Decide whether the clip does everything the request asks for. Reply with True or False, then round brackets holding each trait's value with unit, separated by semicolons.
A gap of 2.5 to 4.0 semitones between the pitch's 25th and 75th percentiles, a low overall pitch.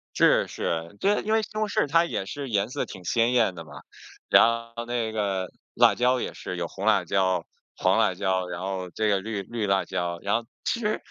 False (4.7 semitones; 100 Hz)